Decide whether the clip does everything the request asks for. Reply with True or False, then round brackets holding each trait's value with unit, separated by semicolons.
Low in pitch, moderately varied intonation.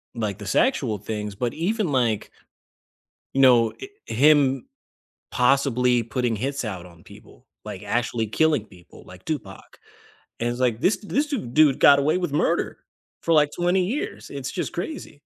False (130 Hz; 5.7 semitones)